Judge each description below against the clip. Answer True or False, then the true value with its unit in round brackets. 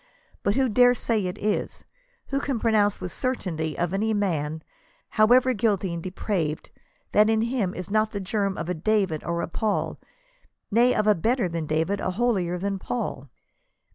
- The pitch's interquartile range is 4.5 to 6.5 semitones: False (4.1 semitones)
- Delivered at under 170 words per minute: False (185 wpm)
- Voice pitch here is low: False (200 Hz)